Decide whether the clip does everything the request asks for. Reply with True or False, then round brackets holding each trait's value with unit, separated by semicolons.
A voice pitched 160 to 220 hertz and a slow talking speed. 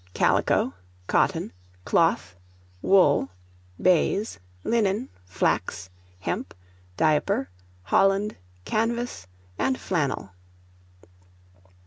True (185 Hz; 65 wpm)